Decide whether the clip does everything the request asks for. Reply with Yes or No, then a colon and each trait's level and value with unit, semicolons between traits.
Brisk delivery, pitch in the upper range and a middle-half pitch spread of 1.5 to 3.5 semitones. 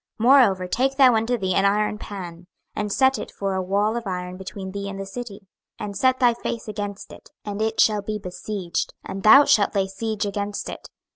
Yes: fast, 215 wpm; high, 205 Hz; narrow, 2.4 semitones